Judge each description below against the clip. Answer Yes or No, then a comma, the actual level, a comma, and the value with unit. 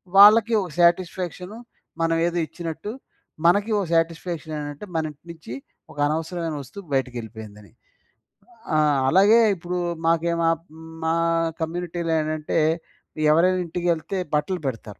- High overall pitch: No, medium, 165 Hz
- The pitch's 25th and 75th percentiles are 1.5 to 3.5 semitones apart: Yes, average, 2.7 semitones